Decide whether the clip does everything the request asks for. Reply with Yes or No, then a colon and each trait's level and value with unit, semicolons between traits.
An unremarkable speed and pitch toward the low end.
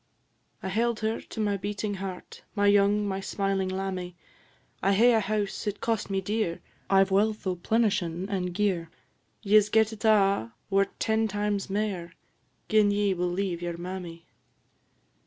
No: average, 170 wpm; high, 200 Hz